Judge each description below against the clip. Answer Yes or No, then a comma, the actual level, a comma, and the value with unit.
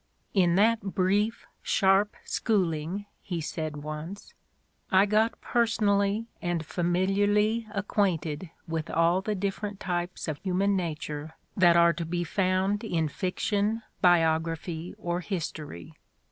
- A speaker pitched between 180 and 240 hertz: Yes, medium, 185 Hz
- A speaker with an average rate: No, slow, 120 wpm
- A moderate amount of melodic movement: Yes, average, 3.6 semitones